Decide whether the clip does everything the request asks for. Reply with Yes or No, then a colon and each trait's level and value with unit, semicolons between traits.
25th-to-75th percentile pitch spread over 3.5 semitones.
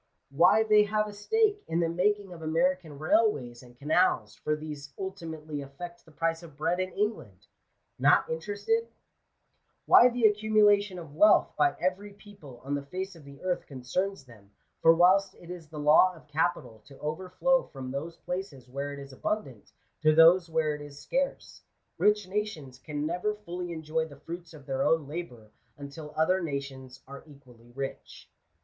Yes: average, 5.1 semitones